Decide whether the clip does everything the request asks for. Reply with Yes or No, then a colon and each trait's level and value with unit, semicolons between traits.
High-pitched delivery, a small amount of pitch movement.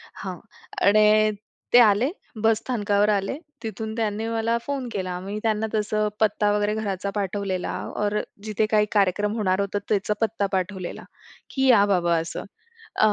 Yes: high, 210 Hz; narrow, 1.7 semitones